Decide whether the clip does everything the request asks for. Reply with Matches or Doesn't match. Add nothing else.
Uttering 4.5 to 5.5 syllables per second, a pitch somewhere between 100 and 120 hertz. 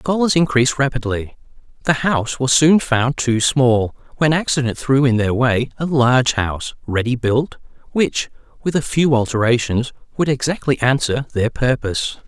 Doesn't match